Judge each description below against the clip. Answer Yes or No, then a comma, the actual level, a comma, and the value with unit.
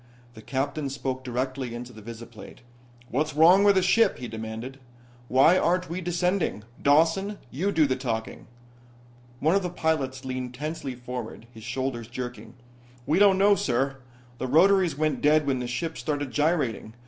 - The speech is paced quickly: No, average, 160 wpm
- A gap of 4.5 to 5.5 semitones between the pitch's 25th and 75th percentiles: Yes, average, 5.1 semitones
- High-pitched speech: No, low, 135 Hz